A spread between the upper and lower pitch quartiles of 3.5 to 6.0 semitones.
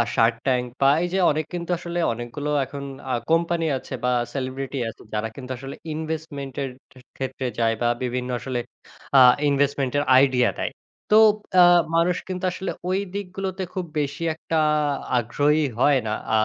Yes: average, 4.6 semitones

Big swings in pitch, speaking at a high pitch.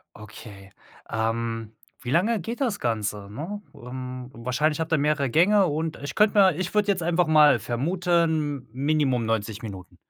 No: wide, 6.9 semitones; medium, 145 Hz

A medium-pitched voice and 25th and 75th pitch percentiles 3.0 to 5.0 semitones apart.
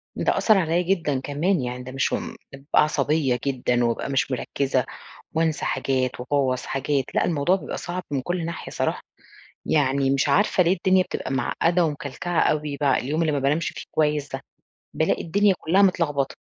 Yes: medium, 145 Hz; average, 4.0 semitones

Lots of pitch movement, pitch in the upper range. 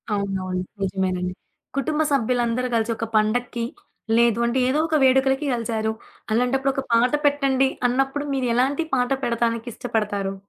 No: average, 3.4 semitones; high, 240 Hz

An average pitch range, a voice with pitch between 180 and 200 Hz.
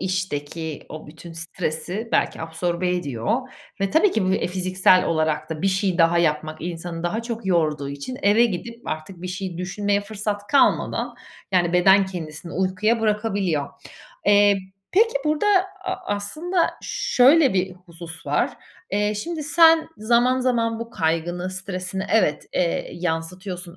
Yes: average, 4.6 semitones; medium, 185 Hz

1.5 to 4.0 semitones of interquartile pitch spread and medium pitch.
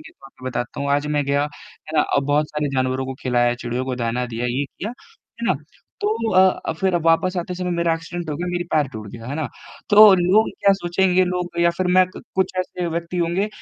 No: average, 5.3 semitones; medium, 165 Hz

